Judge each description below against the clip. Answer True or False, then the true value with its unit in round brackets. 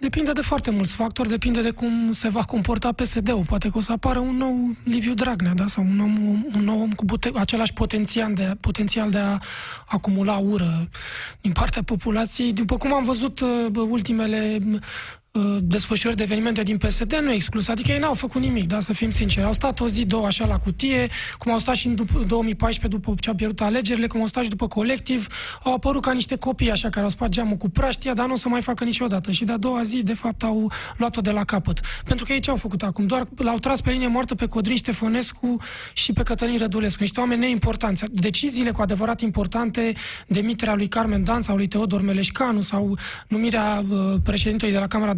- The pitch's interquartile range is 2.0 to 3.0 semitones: True (2.6 semitones)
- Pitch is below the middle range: False (225 Hz)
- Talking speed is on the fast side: True (215 wpm)